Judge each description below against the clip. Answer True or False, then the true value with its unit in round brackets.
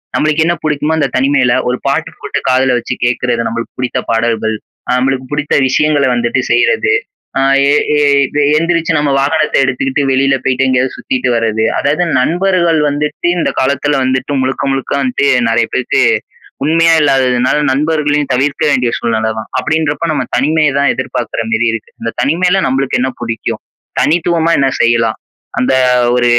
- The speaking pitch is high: False (135 Hz)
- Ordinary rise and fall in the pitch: True (3.4 semitones)